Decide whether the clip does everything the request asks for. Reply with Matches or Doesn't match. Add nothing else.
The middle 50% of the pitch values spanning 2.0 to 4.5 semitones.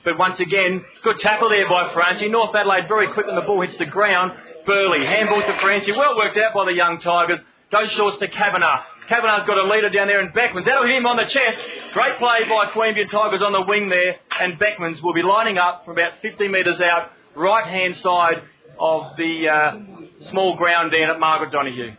Matches